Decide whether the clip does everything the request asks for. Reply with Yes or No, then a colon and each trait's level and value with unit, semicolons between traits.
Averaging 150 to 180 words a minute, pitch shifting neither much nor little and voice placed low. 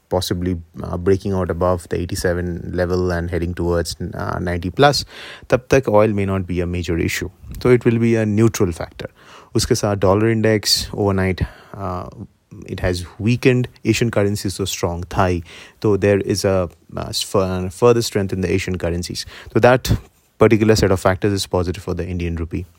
Yes: average, 175 wpm; average, 3.1 semitones; very low, 95 Hz